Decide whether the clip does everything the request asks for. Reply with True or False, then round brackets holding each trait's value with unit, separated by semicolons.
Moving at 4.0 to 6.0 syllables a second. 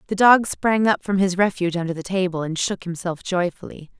True (5.6 syllables/s)